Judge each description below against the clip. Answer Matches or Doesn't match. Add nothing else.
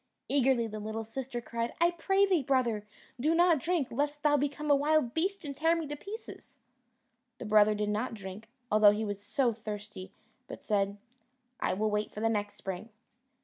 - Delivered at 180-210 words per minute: Matches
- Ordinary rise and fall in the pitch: Doesn't match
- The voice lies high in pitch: Matches